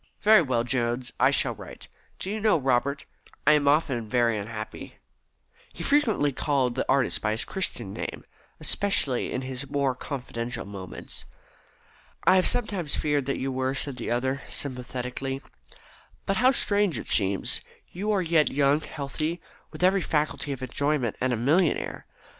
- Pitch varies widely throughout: No, average, 4.5 semitones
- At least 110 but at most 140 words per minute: No, average, 165 wpm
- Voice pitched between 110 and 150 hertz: Yes, medium, 140 Hz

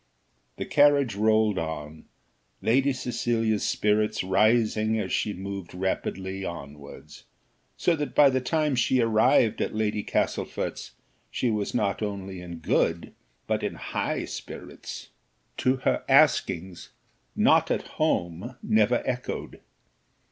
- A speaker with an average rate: No, slow, 120 wpm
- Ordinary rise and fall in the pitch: Yes, average, 4.5 semitones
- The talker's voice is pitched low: Yes, low, 110 Hz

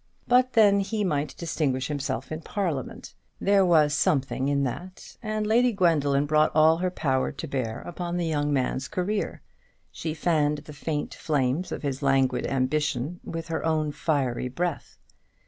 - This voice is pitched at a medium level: Yes, medium, 155 Hz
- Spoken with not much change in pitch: No, average, 4.2 semitones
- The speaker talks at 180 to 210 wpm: No, average, 160 wpm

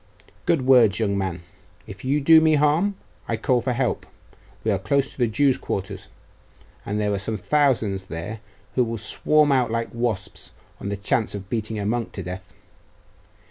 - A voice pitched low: Yes, low, 115 Hz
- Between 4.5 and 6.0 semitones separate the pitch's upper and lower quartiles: Yes, average, 4.9 semitones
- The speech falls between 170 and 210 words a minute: Yes, average, 180 wpm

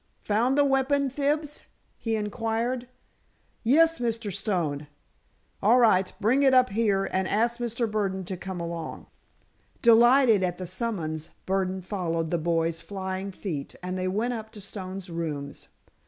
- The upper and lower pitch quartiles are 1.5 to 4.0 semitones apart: No, average, 4.6 semitones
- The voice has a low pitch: No, high, 205 Hz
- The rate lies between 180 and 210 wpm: No, average, 145 wpm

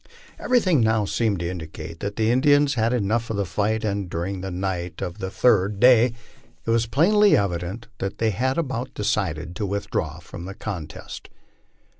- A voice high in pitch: No, low, 105 Hz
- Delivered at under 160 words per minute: No, average, 180 wpm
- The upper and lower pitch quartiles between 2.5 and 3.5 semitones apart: No, average, 4.3 semitones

